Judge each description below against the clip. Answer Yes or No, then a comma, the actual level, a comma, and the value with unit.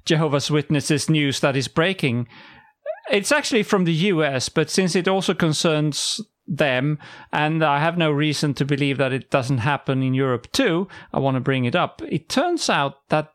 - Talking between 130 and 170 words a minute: No, average, 185 wpm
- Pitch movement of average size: Yes, average, 4.0 semitones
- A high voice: No, medium, 155 Hz